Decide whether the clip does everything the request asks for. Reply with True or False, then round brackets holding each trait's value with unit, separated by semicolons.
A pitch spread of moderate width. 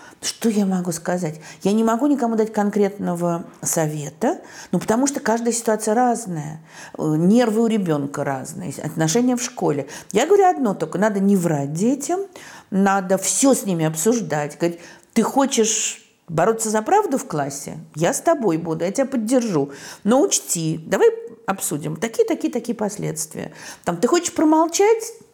False (6.7 semitones)